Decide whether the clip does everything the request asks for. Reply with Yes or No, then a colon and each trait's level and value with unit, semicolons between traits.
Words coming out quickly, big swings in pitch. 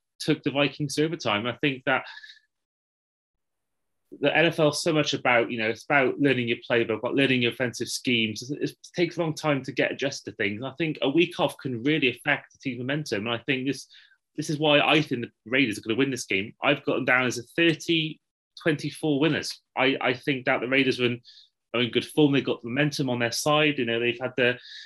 No: fast, 230 wpm; average, 4.0 semitones